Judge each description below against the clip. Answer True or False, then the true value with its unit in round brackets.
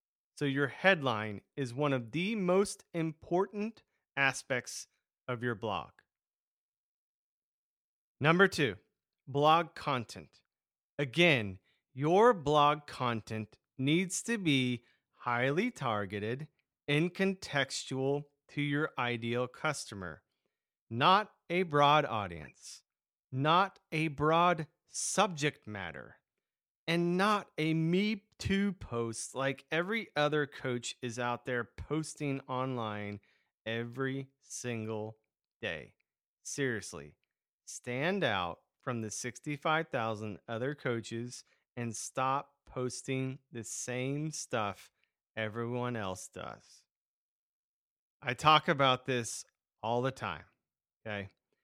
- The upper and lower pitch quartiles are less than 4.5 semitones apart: False (4.9 semitones)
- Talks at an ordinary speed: False (100 wpm)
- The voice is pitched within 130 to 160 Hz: True (135 Hz)